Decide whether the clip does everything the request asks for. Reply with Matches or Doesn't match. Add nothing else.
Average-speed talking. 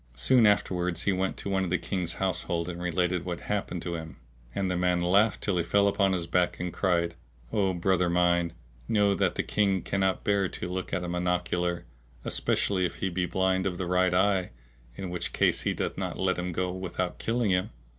Doesn't match